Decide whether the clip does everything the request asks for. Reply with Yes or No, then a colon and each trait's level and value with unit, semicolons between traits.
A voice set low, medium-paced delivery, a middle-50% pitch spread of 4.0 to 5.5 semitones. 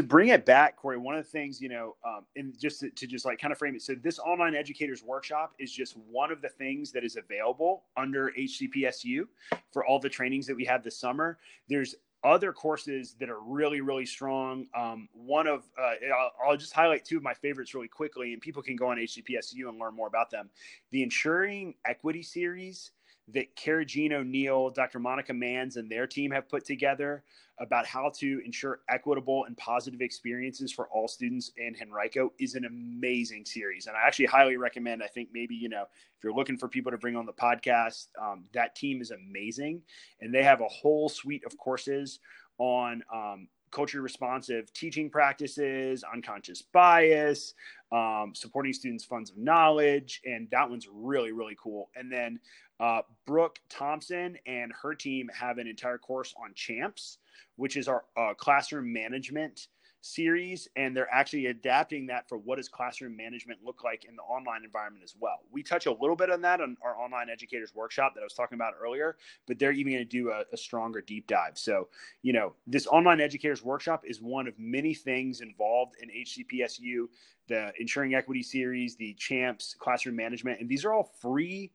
No: low, 130 Hz; average, 190 wpm; average, 3.3 semitones